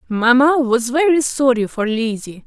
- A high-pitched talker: Yes, very high, 250 Hz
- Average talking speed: Yes, average, 145 wpm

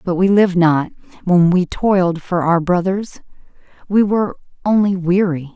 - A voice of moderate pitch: Yes, medium, 180 Hz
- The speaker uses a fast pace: No, average, 150 wpm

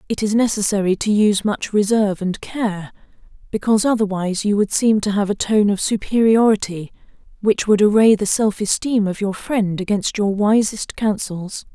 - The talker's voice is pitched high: Yes, high, 205 Hz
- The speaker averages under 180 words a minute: Yes, average, 170 wpm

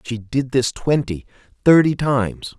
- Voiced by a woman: No, male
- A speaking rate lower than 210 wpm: Yes, average, 140 wpm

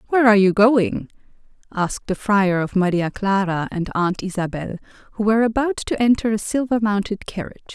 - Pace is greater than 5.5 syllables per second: Yes, 5.7 syllables/s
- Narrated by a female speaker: Yes, female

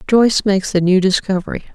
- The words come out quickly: No, average, 170 wpm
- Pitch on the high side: Yes, high, 195 Hz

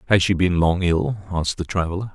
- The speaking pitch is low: Yes, very low, 90 Hz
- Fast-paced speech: Yes, fast, 225 wpm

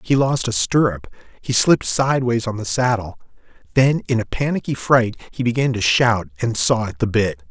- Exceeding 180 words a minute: Yes, average, 190 wpm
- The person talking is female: No, male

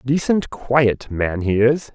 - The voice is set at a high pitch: No, low, 125 Hz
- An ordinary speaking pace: Yes, average, 155 wpm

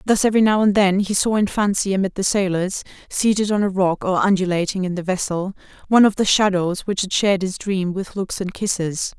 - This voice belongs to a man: No, female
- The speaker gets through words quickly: Yes, fast, 220 wpm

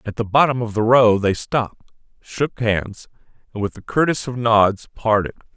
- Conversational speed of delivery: Yes, average, 185 wpm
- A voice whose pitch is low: Yes, low, 115 Hz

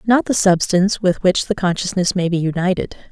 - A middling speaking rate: Yes, average, 195 wpm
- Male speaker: No, female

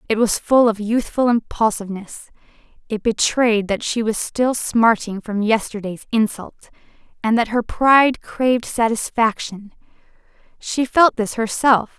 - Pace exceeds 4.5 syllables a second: No, 4.4 syllables/s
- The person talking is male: No, female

